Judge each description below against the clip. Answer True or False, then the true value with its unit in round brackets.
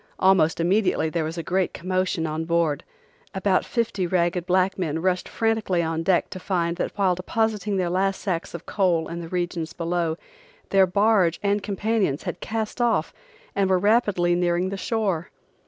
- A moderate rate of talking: True (170 wpm)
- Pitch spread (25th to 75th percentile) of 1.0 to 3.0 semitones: True (2.7 semitones)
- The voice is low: False (185 Hz)